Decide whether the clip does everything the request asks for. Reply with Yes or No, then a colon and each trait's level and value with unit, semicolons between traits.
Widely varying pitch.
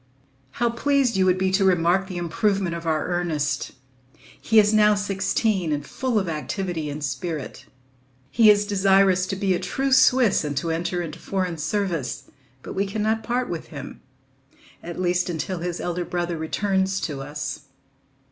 No: average, 3.6 semitones